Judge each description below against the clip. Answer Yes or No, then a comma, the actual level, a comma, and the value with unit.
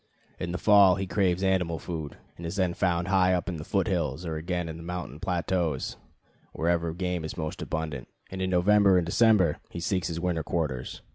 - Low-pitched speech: Yes, very low, 90 Hz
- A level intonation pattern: Yes, narrow, 2.3 semitones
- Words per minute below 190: No, fast, 205 wpm